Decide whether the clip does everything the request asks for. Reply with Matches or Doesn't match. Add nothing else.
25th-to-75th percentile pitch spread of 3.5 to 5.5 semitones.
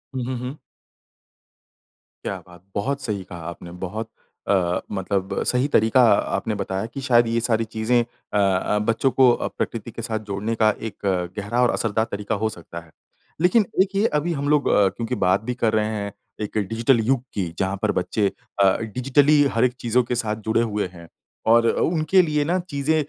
Matches